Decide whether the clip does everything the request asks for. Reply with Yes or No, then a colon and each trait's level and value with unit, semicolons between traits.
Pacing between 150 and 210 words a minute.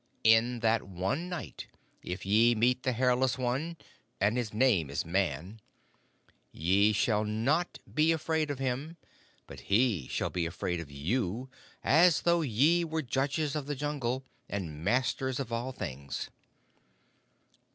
No: average, 140 wpm